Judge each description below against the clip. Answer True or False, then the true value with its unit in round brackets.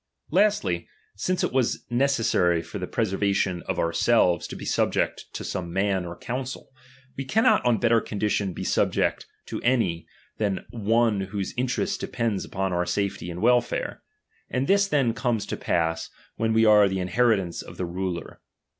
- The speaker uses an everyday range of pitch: True (5.0 semitones)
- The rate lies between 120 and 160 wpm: False (175 wpm)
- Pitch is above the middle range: False (105 Hz)